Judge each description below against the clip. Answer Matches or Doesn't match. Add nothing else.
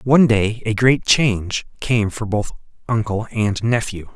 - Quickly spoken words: Doesn't match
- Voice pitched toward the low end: Matches